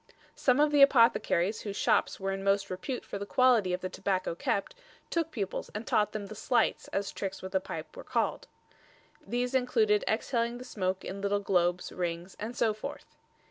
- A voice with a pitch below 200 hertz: No, high, 205 Hz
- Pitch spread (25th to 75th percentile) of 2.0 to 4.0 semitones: No, average, 4.7 semitones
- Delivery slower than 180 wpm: No, average, 190 wpm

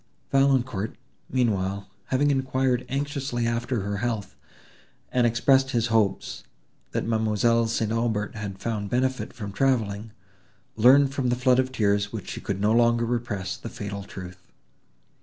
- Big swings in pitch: No, average, 3.7 semitones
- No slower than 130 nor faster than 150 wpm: Yes, average, 140 wpm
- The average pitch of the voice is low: Yes, low, 115 Hz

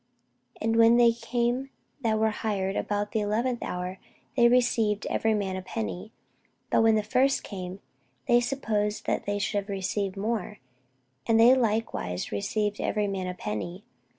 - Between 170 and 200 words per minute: No, average, 160 wpm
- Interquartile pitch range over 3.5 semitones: No, average, 3.0 semitones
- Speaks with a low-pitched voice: No, high, 210 Hz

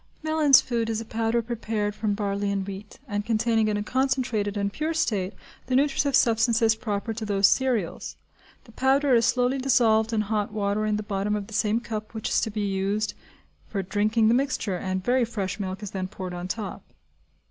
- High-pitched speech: Yes, high, 215 Hz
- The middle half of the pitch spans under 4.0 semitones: Yes, average, 2.8 semitones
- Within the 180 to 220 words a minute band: Yes, average, 200 wpm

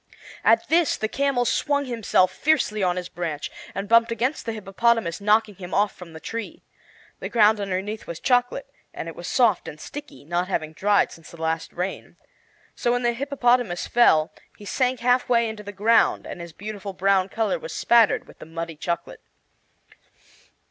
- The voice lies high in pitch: Yes, high, 210 Hz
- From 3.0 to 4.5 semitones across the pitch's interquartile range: No, average, 5.1 semitones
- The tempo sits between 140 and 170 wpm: No, average, 180 wpm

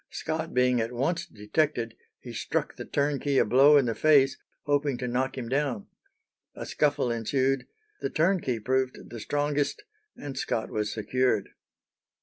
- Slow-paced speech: No, average, 150 wpm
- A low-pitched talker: Yes, low, 130 Hz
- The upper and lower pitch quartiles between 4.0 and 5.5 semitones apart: No, average, 3.3 semitones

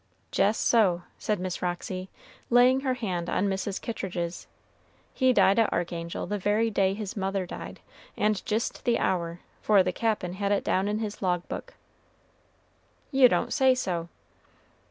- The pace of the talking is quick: No, average, 155 wpm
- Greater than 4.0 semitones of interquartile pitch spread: No, average, 3.5 semitones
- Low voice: No, high, 200 Hz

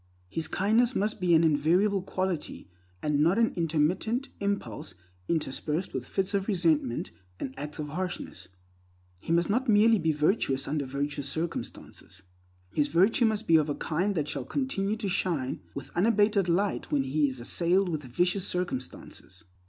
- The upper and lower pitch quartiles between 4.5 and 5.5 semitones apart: Yes, average, 5.2 semitones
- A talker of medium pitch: Yes, medium, 170 Hz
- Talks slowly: No, average, 160 wpm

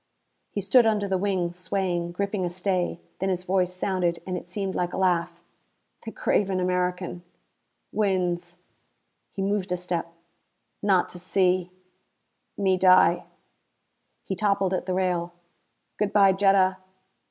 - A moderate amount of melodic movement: No, narrow, 1.6 semitones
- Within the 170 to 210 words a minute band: No, average, 140 wpm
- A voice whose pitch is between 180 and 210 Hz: Yes, medium, 185 Hz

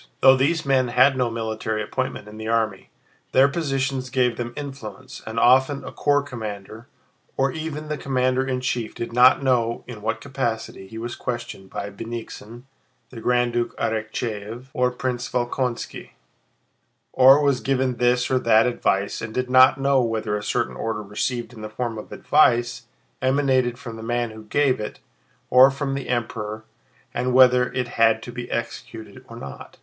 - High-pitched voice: No, low, 125 Hz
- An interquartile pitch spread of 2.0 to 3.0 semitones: Yes, narrow, 2.6 semitones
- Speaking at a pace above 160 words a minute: Yes, average, 170 wpm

